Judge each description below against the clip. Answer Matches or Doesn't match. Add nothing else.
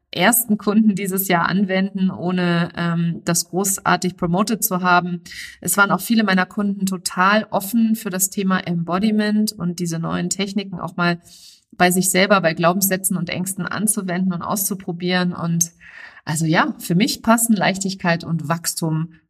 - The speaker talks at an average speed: Matches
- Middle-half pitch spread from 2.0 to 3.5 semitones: Matches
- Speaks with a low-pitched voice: Doesn't match